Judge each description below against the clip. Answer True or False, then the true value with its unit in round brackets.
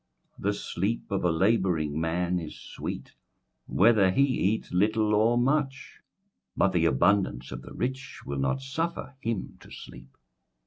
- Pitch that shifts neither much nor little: False (6.3 semitones)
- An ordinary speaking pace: True (150 wpm)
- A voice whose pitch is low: True (100 Hz)